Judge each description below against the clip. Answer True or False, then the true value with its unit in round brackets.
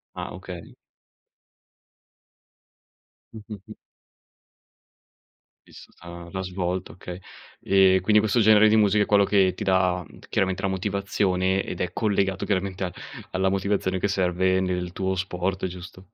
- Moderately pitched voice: False (95 Hz)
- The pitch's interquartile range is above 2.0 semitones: False (1.4 semitones)